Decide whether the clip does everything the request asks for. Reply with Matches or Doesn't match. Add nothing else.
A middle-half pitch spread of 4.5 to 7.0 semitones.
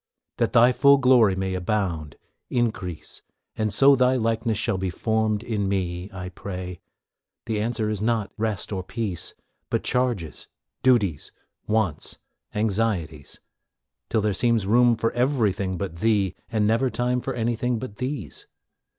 Doesn't match